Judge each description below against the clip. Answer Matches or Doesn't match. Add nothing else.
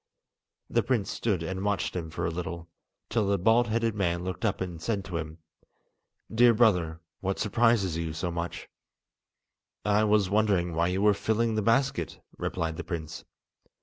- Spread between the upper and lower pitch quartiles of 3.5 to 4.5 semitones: Matches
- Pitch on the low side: Matches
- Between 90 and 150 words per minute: Doesn't match